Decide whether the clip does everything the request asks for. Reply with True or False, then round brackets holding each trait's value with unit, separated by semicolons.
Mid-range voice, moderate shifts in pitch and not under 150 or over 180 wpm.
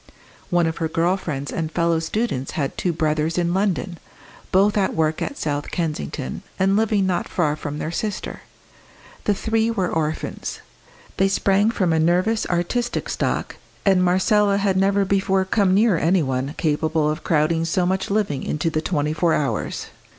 True (175 Hz; 3.8 semitones; 170 wpm)